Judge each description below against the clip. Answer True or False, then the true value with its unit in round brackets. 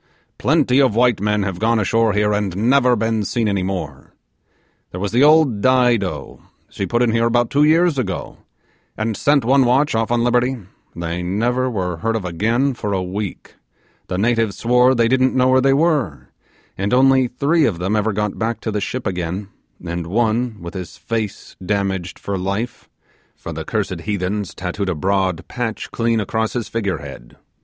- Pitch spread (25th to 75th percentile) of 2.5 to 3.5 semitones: False (4.2 semitones)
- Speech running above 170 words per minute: True (185 wpm)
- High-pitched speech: False (110 Hz)